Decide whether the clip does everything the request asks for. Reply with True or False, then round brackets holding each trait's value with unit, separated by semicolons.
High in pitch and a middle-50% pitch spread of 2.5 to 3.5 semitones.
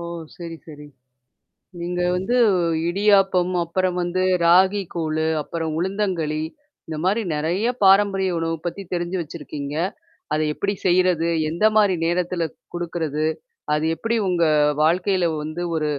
False (175 Hz; 2.8 semitones)